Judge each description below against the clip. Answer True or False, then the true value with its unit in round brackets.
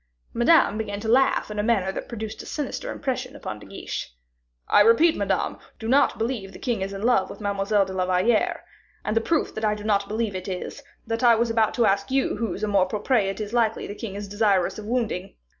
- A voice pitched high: True (215 Hz)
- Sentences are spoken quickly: True (235 wpm)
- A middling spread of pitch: True (3.0 semitones)